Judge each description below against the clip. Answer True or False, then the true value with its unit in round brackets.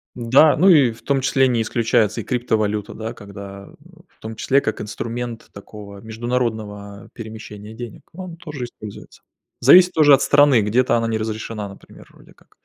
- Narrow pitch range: False (3.3 semitones)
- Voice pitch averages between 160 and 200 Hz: False (115 Hz)